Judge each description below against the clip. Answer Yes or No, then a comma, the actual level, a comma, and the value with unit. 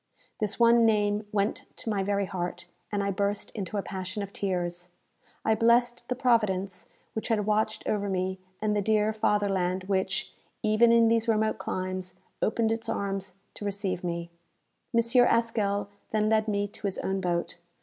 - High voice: Yes, high, 205 Hz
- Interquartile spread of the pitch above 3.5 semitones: No, narrow, 2.5 semitones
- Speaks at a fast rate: No, average, 170 wpm